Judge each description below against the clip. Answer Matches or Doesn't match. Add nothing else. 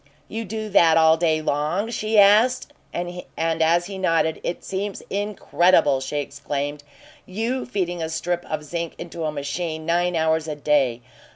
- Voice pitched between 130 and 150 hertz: Doesn't match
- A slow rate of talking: Doesn't match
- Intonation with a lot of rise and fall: Doesn't match